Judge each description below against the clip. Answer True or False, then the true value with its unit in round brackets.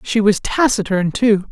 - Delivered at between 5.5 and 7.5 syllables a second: False (4.4 syllables/s)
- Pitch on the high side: True (210 Hz)